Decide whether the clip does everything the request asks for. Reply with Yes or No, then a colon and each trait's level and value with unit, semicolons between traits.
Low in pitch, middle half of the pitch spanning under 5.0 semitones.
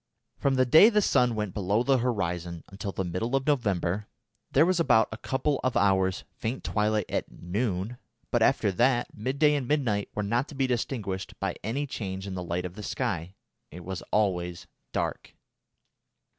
No: low, 105 Hz; wide, 5.5 semitones